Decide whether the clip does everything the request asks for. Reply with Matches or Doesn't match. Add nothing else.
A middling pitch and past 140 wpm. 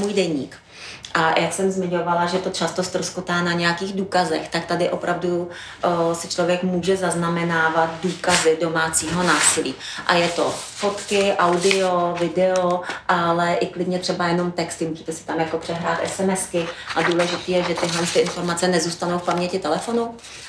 Matches